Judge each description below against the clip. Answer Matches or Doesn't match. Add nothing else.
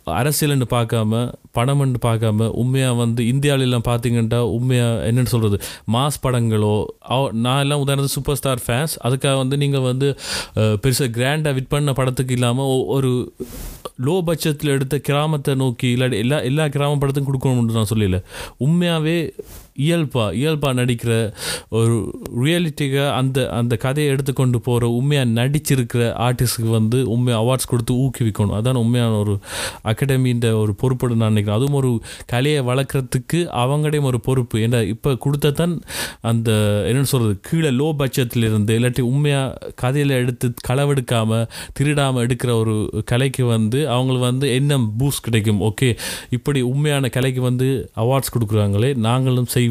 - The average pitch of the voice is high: Doesn't match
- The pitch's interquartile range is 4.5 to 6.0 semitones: Doesn't match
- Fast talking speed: Matches